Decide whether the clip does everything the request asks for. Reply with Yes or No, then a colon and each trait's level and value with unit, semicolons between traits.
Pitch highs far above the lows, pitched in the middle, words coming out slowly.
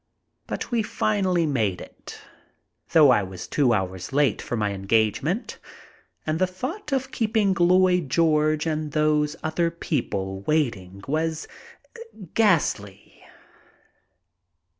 Yes: wide, 8.6 semitones; medium, 155 Hz; slow, 120 wpm